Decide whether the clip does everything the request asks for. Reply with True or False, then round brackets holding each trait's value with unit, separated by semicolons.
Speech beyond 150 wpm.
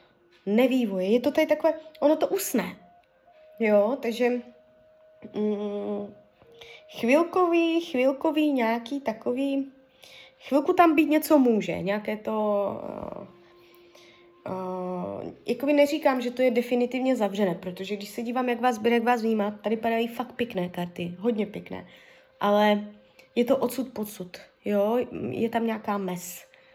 False (130 wpm)